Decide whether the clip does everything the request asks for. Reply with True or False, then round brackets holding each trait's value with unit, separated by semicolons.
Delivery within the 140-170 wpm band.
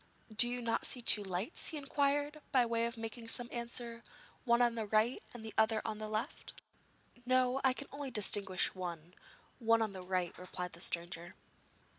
False (185 wpm)